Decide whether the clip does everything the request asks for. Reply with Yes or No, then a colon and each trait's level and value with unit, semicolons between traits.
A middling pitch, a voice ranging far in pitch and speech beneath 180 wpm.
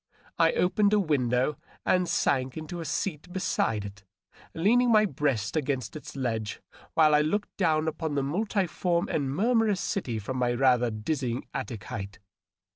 Yes: medium, 150 Hz; wide, 6.5 semitones; average, 155 wpm